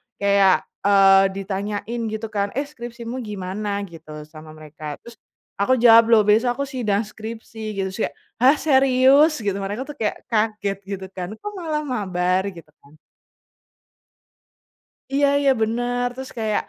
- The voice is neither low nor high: No, high, 215 Hz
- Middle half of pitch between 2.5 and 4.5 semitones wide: Yes, average, 4.1 semitones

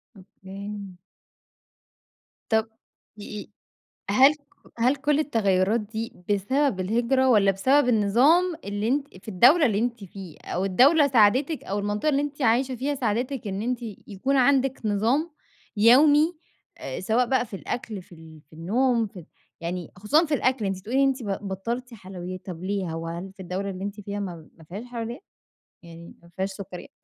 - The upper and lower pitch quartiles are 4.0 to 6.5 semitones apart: Yes, average, 5.2 semitones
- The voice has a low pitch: No, high, 215 Hz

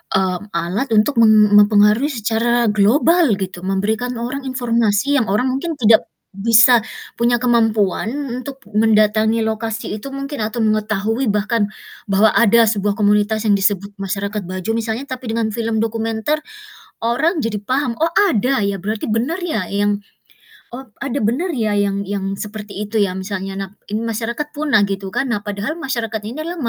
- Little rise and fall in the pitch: No, average, 3.1 semitones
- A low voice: No, high, 220 Hz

